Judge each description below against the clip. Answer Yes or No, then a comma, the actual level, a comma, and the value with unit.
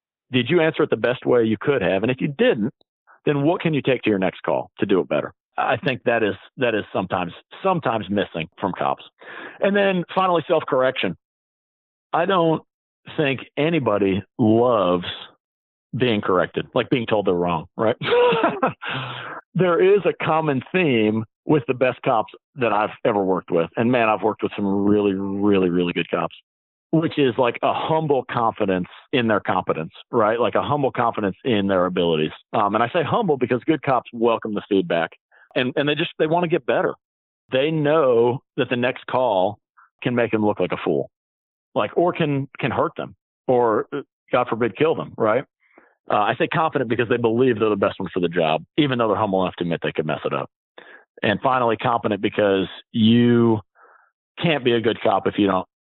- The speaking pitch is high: No, low, 120 Hz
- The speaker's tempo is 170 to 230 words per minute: Yes, average, 195 wpm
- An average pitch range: No, wide, 7.2 semitones